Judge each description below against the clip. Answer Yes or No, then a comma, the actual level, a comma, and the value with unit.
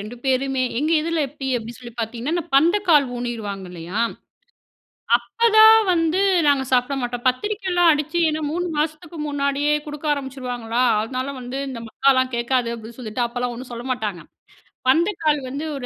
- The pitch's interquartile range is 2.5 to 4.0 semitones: No, average, 4.4 semitones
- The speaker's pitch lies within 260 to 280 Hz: Yes, very high, 265 Hz